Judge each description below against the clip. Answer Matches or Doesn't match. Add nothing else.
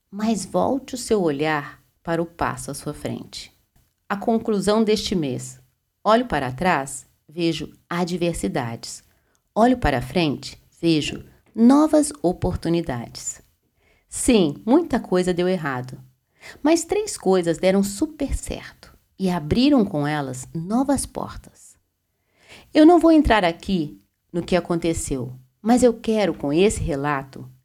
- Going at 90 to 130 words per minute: Matches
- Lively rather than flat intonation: Matches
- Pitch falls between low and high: Matches